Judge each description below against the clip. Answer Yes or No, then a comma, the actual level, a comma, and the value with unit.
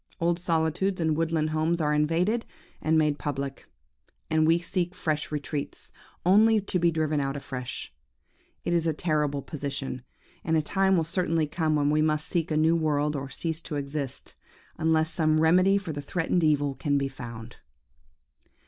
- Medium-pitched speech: Yes, medium, 155 Hz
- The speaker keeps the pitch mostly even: Yes, narrow, 2.3 semitones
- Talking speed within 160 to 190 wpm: Yes, average, 170 wpm